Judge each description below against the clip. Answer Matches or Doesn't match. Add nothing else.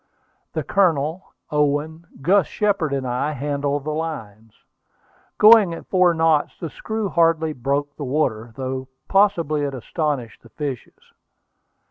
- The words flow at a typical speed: Doesn't match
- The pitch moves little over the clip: Doesn't match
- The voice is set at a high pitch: Doesn't match